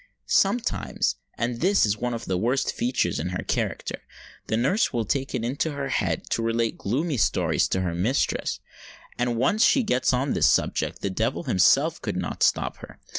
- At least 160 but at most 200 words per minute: Yes, average, 180 wpm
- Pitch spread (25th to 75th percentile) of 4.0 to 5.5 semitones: Yes, average, 4.5 semitones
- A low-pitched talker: Yes, low, 120 Hz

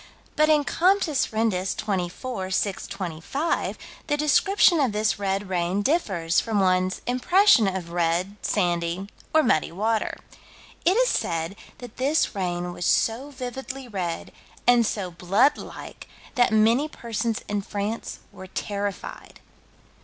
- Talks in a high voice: Yes, high, 210 Hz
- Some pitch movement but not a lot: No, wide, 5.9 semitones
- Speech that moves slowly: Yes, slow, 130 wpm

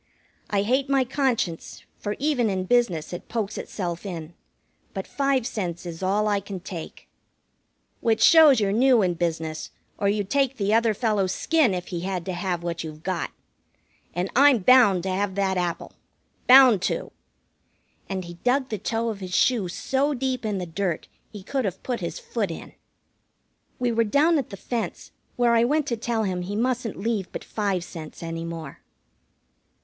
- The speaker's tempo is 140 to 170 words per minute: No, average, 180 wpm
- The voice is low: No, high, 205 Hz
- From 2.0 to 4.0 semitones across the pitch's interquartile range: No, average, 5.3 semitones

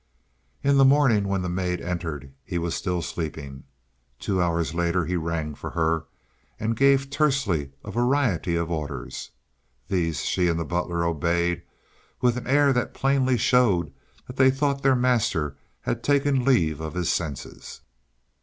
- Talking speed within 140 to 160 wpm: Yes, average, 155 wpm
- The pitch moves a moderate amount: No, wide, 7.5 semitones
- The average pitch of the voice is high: No, very low, 90 Hz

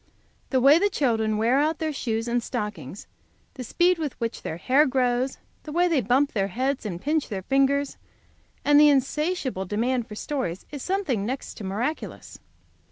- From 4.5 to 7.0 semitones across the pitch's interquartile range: Yes, average, 5.1 semitones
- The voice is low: No, very high, 260 Hz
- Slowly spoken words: No, average, 175 wpm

